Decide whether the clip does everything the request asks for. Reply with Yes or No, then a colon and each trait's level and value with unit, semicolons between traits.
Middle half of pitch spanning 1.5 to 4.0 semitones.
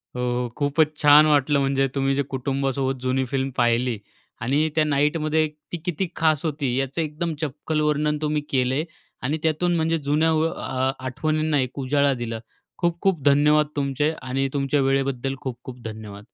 Yes: average, 2.7 semitones